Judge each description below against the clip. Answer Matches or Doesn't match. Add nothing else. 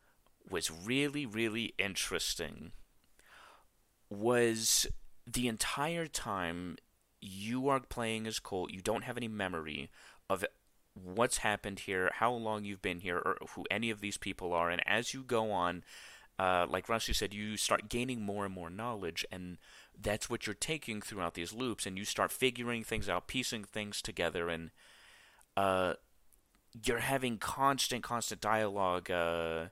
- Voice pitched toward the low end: Matches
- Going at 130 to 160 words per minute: Matches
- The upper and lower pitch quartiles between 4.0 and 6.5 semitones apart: Matches